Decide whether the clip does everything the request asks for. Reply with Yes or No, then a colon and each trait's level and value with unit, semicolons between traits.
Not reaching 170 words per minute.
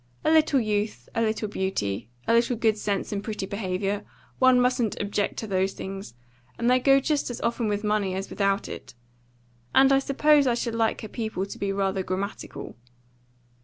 No: average, 185 wpm